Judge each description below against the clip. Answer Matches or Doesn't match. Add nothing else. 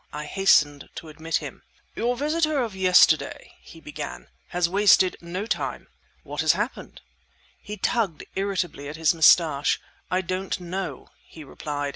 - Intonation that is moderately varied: Matches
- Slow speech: Doesn't match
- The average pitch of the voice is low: Doesn't match